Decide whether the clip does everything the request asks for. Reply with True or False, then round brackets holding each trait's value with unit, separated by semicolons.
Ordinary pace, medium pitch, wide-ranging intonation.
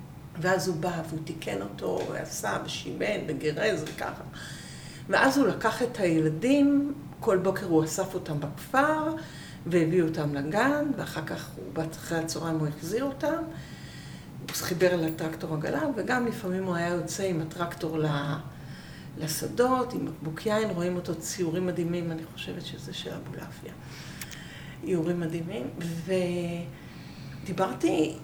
False (130 wpm; 170 Hz; 3.5 semitones)